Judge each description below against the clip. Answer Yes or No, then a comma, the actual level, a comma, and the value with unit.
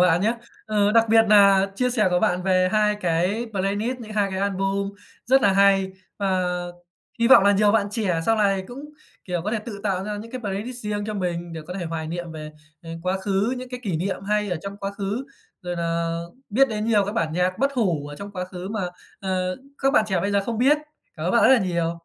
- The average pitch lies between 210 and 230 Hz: No, high, 200 Hz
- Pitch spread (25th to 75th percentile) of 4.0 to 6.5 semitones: No, average, 2.9 semitones